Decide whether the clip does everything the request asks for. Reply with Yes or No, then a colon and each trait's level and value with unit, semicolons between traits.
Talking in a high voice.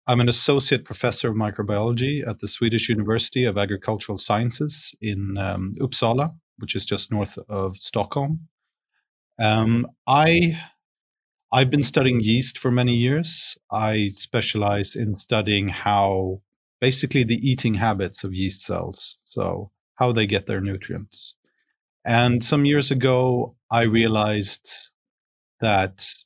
No: low, 115 Hz